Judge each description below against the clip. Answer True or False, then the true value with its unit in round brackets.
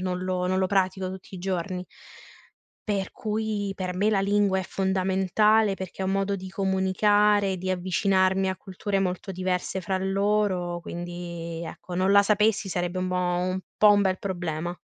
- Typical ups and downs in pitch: False (1.5 semitones)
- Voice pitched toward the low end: False (190 Hz)